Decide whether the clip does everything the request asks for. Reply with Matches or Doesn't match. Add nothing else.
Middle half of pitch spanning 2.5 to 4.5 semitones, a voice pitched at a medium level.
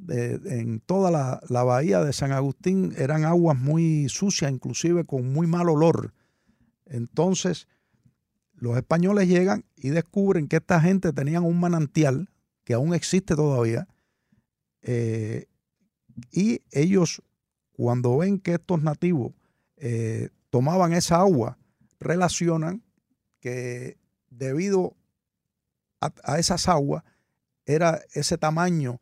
Doesn't match